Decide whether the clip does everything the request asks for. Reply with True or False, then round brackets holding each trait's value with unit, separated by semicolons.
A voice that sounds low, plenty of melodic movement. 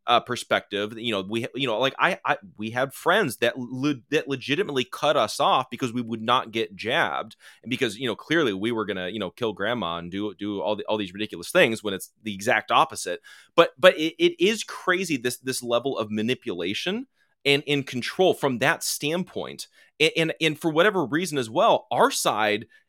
True (130 Hz; 6.4 semitones)